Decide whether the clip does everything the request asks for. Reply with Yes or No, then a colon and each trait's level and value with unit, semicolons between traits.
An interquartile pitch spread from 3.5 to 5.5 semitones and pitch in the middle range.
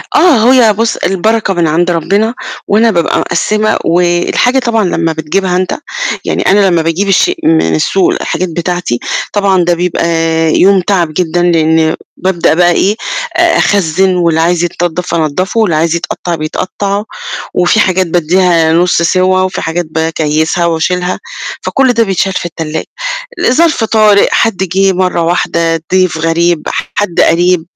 No: average, 2.9 semitones; medium, 180 Hz